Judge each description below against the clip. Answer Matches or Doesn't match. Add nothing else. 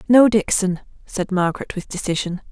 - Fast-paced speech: Doesn't match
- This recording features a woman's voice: Matches